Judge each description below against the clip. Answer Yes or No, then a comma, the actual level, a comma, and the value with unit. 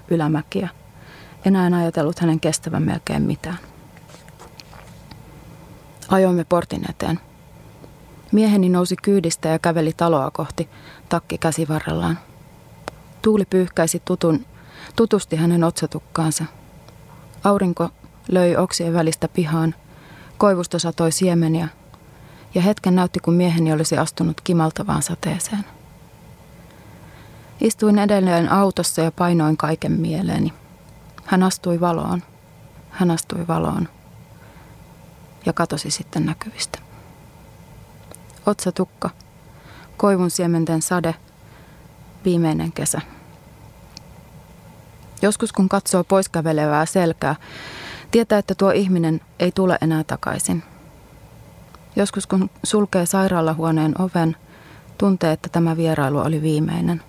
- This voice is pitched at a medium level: Yes, medium, 170 Hz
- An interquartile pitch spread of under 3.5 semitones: Yes, average, 2.8 semitones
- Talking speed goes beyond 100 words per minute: No, slow, 95 wpm